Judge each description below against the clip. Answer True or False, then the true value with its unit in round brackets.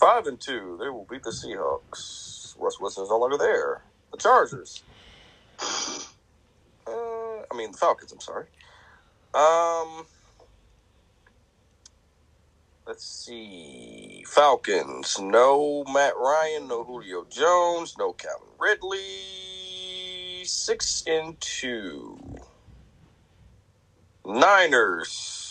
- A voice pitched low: False (160 Hz)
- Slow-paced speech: True (95 wpm)